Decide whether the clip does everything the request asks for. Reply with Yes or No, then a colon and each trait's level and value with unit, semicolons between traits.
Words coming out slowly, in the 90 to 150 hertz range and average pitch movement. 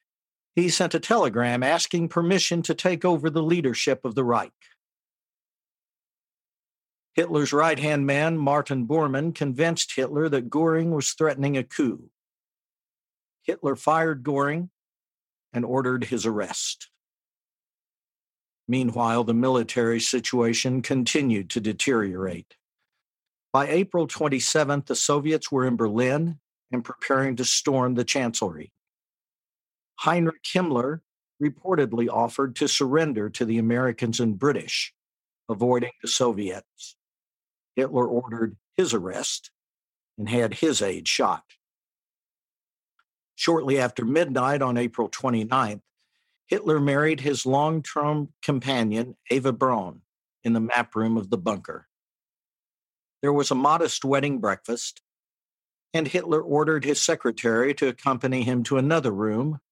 Yes: slow, 115 wpm; low, 135 Hz; average, 4.3 semitones